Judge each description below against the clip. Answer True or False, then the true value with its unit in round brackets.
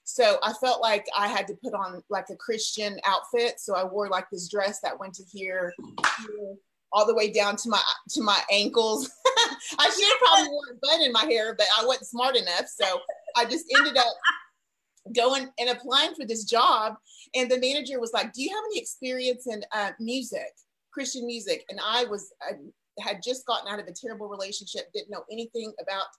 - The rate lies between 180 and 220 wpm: True (205 wpm)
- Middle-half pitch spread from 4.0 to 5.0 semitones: True (4.3 semitones)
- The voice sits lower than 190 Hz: False (230 Hz)